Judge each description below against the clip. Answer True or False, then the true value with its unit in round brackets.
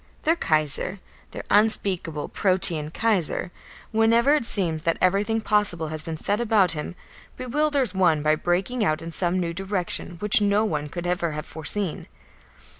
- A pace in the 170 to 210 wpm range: False (155 wpm)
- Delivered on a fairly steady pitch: False (4.6 semitones)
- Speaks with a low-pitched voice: False (185 Hz)